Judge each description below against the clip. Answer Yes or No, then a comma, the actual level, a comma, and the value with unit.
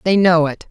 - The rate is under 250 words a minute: No, fast, 255 wpm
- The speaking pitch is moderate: Yes, medium, 170 Hz